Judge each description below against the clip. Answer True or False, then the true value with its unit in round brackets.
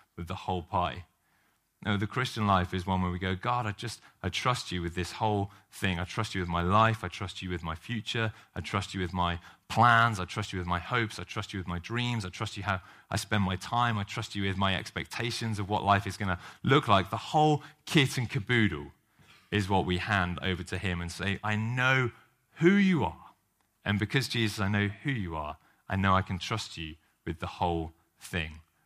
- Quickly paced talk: True (235 wpm)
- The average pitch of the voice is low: True (100 Hz)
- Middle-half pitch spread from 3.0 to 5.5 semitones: True (3.8 semitones)